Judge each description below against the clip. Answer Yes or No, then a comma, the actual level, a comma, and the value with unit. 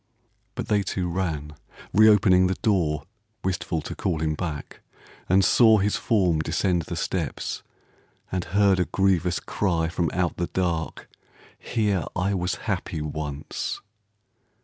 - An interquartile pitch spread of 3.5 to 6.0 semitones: No, average, 3.1 semitones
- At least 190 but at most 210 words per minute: No, average, 140 wpm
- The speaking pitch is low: Yes, very low, 90 Hz